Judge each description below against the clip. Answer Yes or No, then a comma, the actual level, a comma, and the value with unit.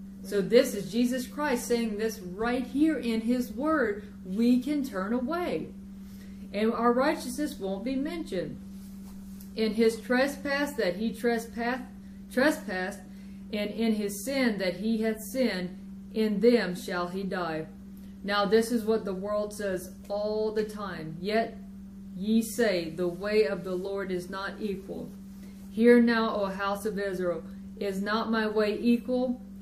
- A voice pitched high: Yes, high, 210 Hz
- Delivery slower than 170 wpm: Yes, average, 150 wpm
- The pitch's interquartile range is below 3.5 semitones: Yes, average, 3.1 semitones